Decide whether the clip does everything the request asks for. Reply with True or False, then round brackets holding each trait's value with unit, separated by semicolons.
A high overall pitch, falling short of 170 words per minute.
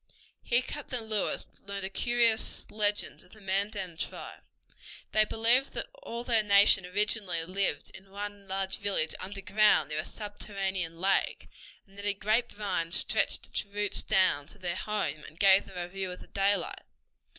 True (200 Hz; 160 wpm)